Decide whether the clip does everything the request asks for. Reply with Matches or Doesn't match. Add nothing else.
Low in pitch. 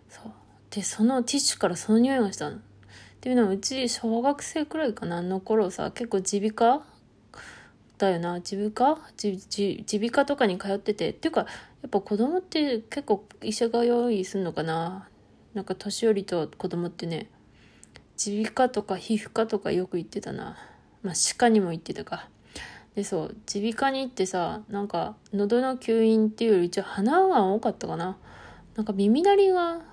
Doesn't match